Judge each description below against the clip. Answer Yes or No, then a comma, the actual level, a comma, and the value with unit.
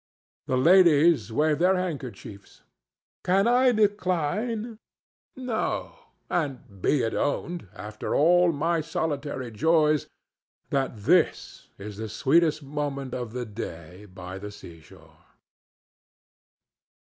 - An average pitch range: No, wide, 7.8 semitones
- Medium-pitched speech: Yes, medium, 145 Hz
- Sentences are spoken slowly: Yes, slow, 105 wpm